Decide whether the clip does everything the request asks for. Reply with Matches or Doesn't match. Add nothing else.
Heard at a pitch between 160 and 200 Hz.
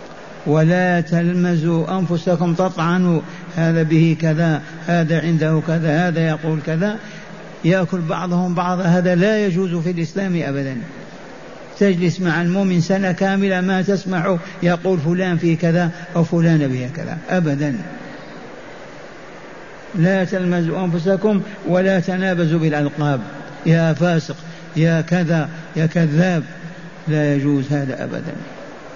Matches